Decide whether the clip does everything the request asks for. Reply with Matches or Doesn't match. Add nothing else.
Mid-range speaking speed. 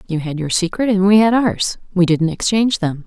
Doesn't match